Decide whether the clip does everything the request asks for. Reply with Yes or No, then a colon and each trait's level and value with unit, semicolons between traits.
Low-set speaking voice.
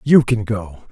Yes: low, 110 Hz